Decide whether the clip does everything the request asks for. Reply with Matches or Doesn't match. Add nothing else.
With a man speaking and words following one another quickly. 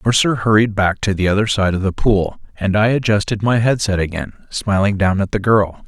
Matches